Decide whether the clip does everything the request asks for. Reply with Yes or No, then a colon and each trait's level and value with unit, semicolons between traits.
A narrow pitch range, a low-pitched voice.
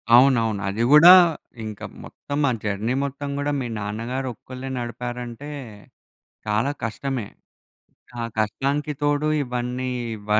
No: average, 3.6 semitones; low, 125 Hz